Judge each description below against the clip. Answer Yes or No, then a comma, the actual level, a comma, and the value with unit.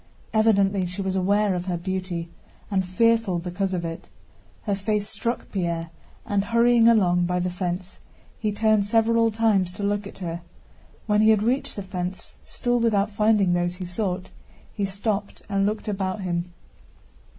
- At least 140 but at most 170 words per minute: Yes, average, 165 wpm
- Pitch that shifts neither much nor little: Yes, average, 3.1 semitones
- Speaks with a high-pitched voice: Yes, high, 195 Hz